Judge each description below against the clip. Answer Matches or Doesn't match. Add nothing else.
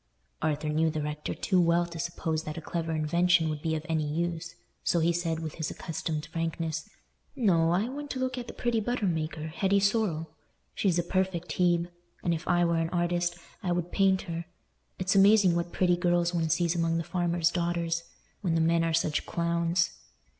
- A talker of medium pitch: Matches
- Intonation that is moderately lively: Doesn't match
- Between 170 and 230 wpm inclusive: Matches